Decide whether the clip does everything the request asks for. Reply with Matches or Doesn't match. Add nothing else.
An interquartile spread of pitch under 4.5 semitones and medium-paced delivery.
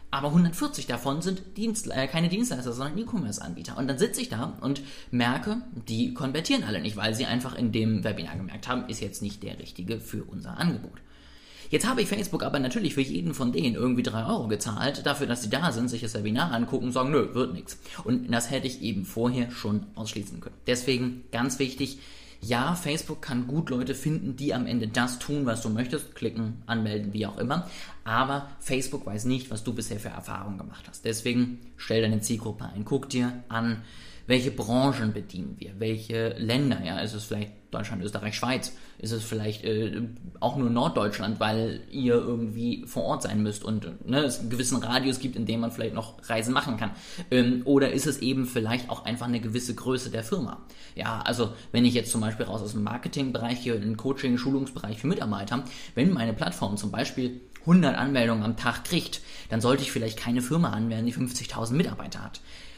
Doesn't match